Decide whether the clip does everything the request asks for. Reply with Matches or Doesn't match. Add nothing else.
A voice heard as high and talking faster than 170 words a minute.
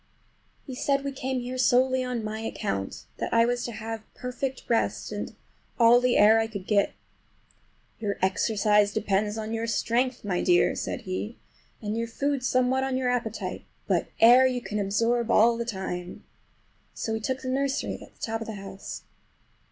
Matches